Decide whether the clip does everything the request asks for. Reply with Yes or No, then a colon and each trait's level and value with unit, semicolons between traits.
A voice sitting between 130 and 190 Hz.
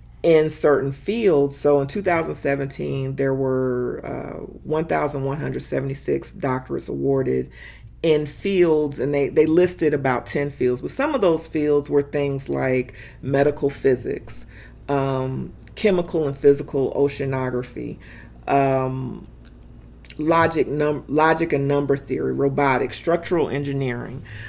Yes: medium, 140 Hz